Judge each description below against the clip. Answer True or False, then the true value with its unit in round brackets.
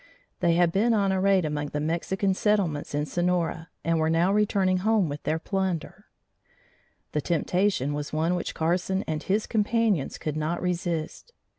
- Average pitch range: True (3.5 semitones)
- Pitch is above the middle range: False (175 Hz)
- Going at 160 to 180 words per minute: True (165 wpm)